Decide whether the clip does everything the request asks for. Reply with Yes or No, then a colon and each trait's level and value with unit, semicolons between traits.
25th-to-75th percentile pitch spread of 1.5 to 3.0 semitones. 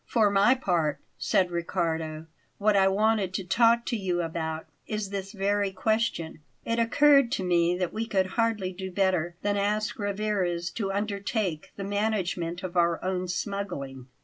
No: average, 3.4 semitones